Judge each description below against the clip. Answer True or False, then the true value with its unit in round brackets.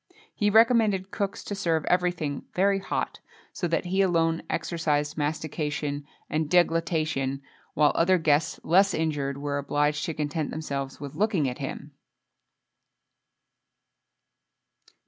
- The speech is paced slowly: True (120 wpm)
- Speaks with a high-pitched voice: False (160 Hz)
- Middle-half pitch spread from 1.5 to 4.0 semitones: True (3.6 semitones)